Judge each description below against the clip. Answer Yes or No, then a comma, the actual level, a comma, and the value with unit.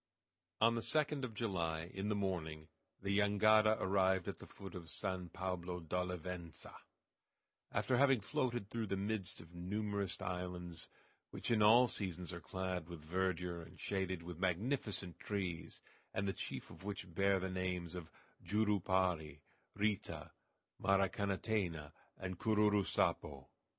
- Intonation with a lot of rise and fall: No, average, 2.8 semitones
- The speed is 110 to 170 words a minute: Yes, average, 140 wpm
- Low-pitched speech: Yes, very low, 95 Hz